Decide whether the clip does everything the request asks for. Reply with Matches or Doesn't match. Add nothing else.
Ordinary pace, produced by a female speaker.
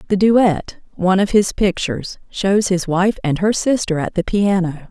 Matches